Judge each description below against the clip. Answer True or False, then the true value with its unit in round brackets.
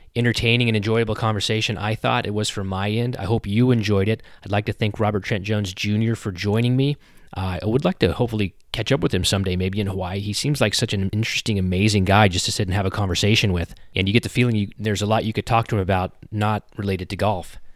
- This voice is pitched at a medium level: False (105 Hz)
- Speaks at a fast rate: True (255 wpm)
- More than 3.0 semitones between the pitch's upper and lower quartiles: False (2.4 semitones)